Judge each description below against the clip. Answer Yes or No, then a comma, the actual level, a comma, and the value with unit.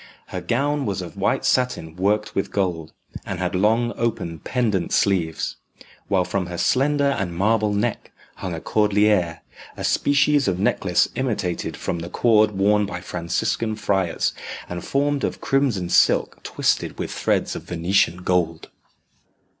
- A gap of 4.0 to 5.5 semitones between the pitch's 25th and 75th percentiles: Yes, average, 4.7 semitones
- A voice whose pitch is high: No, low, 100 Hz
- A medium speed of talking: Yes, average, 145 wpm